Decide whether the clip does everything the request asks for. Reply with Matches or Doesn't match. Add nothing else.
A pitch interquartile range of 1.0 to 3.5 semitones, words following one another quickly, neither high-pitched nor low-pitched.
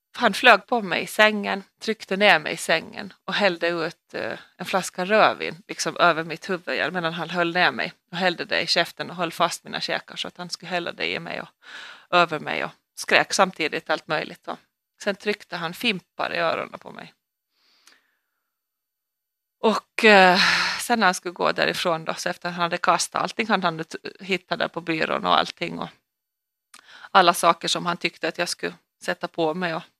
Matches